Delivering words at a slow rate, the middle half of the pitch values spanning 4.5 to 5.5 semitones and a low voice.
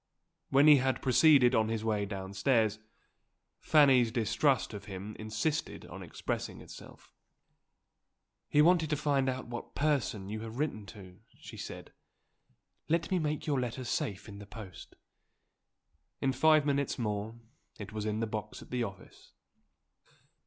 No: average, 145 wpm; average, 5.1 semitones; low, 120 Hz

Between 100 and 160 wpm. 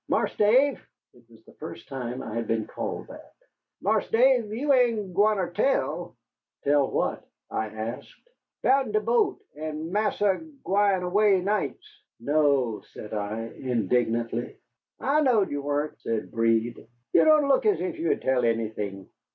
Yes: average, 150 wpm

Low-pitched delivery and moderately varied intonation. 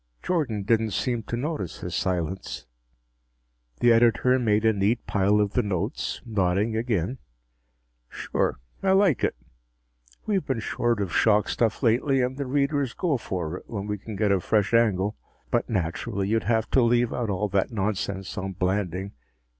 Yes: low, 110 Hz; average, 3.7 semitones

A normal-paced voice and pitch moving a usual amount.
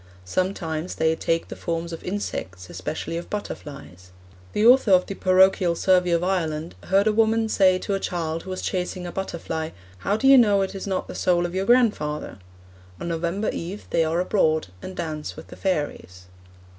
Yes: average, 190 wpm; average, 3.4 semitones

